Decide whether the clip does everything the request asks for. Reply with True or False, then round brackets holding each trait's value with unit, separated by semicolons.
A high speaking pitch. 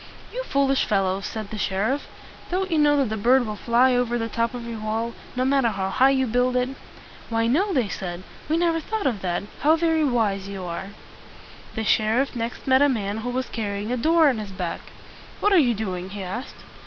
True (235 Hz)